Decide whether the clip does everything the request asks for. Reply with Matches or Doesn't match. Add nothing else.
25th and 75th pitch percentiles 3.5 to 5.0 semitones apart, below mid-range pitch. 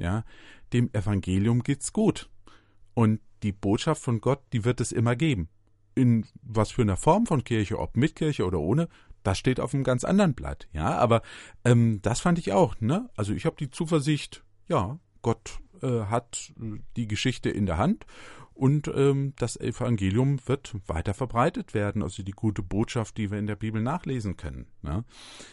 Matches